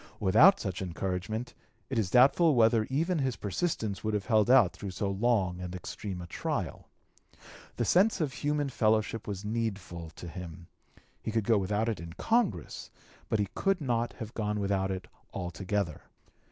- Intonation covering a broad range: No, average, 4.4 semitones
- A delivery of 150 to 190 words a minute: Yes, average, 165 wpm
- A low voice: Yes, low, 105 Hz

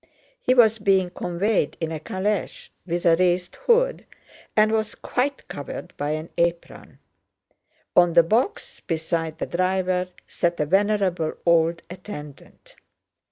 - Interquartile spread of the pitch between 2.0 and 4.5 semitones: Yes, average, 3.8 semitones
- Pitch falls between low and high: Yes, medium, 180 Hz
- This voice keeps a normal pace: No, slow, 130 wpm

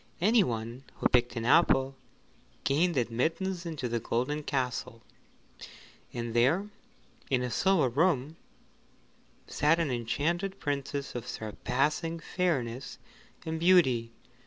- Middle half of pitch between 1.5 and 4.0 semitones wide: No, wide, 5.5 semitones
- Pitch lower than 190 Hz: Yes, medium, 140 Hz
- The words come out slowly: Yes, slow, 110 wpm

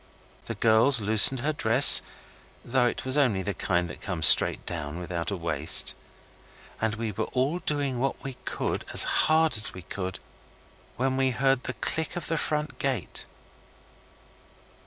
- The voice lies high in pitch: No, low, 120 Hz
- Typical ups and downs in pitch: No, wide, 5.7 semitones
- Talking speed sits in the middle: Yes, average, 160 wpm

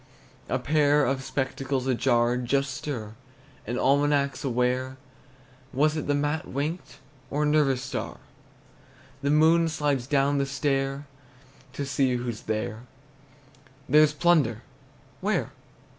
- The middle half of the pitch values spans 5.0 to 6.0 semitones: No, narrow, 2.6 semitones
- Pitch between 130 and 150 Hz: Yes, low, 135 Hz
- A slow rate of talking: Yes, slow, 120 wpm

